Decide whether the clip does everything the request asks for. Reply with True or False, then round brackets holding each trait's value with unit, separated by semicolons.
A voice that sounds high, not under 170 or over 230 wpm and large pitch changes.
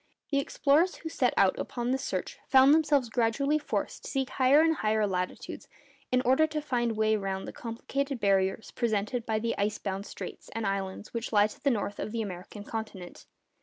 False (230 Hz; 200 wpm; 4.8 semitones)